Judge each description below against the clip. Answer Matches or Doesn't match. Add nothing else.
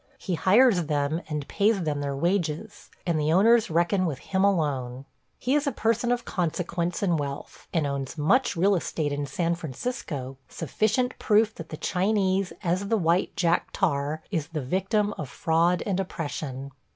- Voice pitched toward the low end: Doesn't match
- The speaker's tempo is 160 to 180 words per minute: Matches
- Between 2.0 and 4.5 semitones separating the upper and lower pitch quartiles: Doesn't match